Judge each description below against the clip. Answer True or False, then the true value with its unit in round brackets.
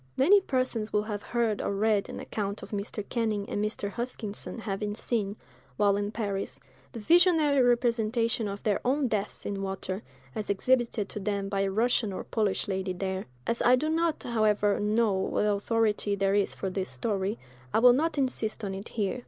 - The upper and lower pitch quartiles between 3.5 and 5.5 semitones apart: False (3.0 semitones)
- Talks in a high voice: True (210 Hz)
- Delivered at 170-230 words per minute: True (185 wpm)